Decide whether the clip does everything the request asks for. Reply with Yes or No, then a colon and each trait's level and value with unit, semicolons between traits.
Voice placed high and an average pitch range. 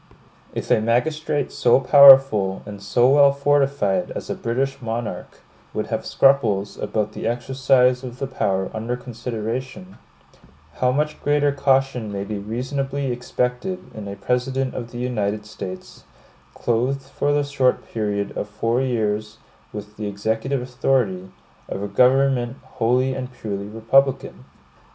No: low, 125 Hz; average, 4.1 semitones